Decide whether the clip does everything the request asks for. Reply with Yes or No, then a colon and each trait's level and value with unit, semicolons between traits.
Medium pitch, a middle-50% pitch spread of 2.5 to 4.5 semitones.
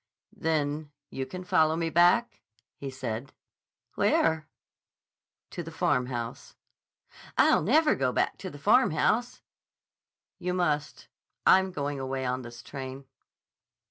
No: medium, 150 Hz; average, 5.1 semitones